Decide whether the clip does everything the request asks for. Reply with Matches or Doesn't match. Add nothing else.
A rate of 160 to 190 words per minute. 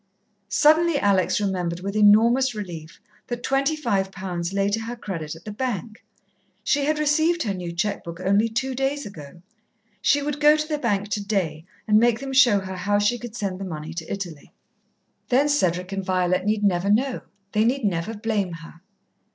Matches